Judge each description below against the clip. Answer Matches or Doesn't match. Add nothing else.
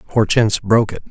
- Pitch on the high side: Doesn't match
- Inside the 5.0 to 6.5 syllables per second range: Matches